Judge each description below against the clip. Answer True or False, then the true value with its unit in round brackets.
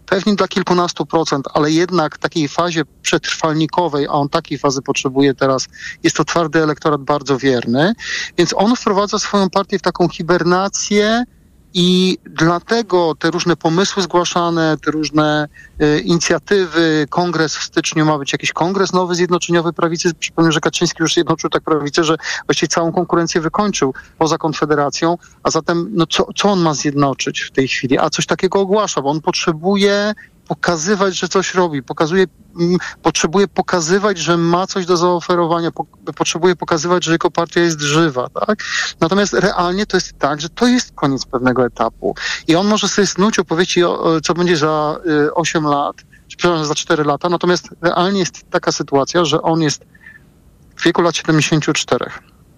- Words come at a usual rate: False (165 wpm)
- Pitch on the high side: False (170 Hz)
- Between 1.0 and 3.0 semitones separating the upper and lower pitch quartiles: True (2.6 semitones)